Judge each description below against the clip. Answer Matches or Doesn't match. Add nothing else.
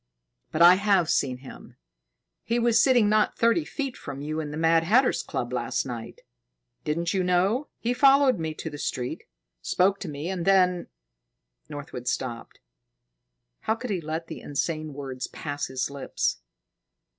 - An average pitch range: Doesn't match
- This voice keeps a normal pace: Matches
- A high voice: Doesn't match